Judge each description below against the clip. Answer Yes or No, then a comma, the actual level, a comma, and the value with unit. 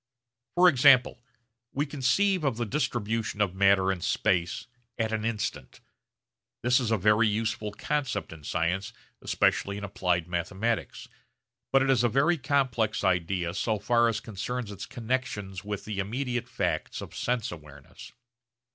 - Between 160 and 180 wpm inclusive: No, average, 145 wpm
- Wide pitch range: No, average, 4.4 semitones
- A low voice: Yes, low, 110 Hz